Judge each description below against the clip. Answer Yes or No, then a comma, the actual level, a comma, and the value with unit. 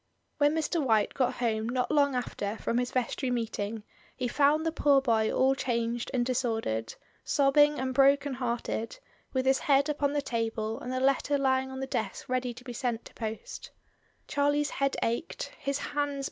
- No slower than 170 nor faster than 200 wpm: Yes, average, 180 wpm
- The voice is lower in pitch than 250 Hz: No, very high, 255 Hz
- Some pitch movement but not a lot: Yes, average, 3.3 semitones